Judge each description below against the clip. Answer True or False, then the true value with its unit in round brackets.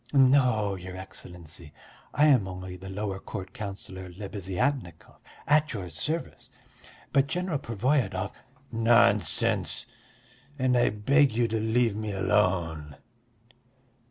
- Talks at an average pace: False (110 wpm)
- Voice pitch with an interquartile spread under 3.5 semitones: False (5.3 semitones)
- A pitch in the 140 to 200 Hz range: False (105 Hz)